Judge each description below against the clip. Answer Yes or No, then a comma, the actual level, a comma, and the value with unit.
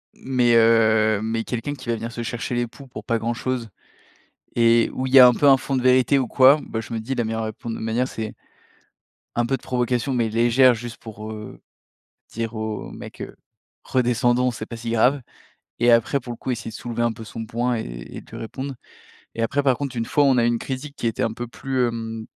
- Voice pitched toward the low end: Yes, low, 120 Hz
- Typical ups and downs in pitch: No, narrow, 2.1 semitones